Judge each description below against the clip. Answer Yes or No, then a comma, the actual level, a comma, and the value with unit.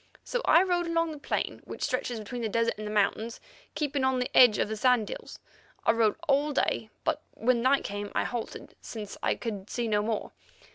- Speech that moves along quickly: Yes, fast, 210 wpm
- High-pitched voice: Yes, high, 235 Hz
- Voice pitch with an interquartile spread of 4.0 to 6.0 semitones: Yes, average, 4.6 semitones